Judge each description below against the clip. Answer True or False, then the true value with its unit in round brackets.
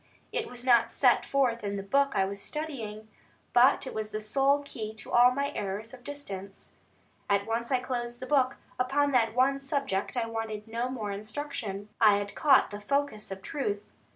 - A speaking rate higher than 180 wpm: True (190 wpm)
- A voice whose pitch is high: True (235 Hz)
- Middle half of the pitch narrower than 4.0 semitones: False (4.5 semitones)